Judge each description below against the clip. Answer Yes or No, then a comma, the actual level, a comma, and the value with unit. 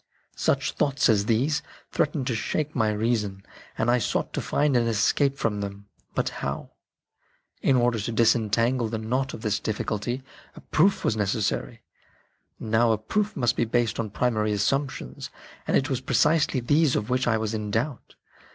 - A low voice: Yes, low, 115 Hz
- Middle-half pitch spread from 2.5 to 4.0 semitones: Yes, average, 3.7 semitones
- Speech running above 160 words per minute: Yes, average, 170 wpm